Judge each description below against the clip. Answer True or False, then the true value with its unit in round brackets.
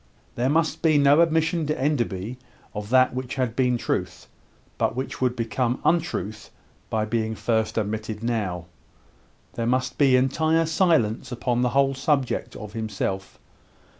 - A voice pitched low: True (125 Hz)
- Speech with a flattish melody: False (4.1 semitones)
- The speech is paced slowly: False (145 wpm)